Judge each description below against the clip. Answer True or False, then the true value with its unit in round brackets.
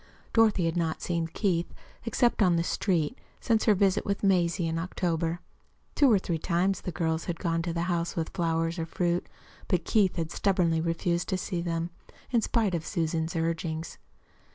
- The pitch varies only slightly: True (2.3 semitones)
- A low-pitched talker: False (170 Hz)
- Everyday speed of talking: True (180 wpm)